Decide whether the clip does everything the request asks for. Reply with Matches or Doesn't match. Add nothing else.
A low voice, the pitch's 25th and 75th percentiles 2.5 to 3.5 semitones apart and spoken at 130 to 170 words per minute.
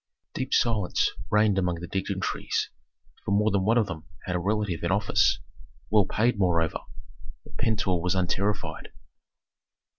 Matches